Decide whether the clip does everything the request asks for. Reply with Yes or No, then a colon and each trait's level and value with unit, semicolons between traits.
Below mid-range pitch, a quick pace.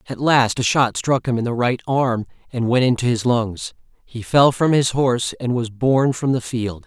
Yes: low, 125 Hz; fast, 235 wpm